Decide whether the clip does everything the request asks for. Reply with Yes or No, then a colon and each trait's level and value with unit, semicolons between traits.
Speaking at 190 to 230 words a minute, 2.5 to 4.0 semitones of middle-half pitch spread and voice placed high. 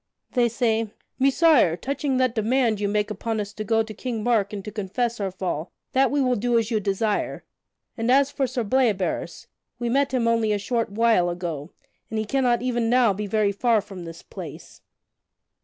Yes: average, 195 wpm; average, 3.2 semitones; high, 225 Hz